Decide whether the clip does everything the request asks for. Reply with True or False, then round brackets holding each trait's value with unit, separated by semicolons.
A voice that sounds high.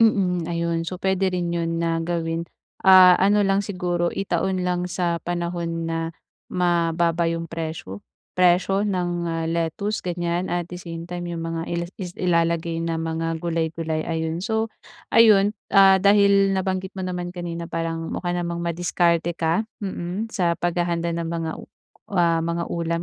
False (175 Hz)